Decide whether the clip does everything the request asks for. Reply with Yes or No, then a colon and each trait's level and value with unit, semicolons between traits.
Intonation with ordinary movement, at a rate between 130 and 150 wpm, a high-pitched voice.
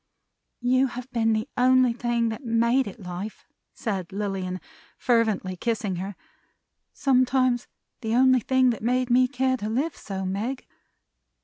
Yes: average, 3.6 semitones; average, 140 wpm; high, 235 Hz